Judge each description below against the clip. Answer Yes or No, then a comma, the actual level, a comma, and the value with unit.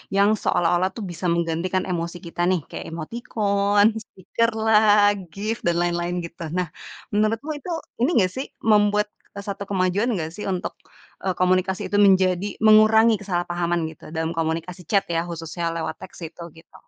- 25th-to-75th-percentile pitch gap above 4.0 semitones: No, average, 3.2 semitones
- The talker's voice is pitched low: No, medium, 185 Hz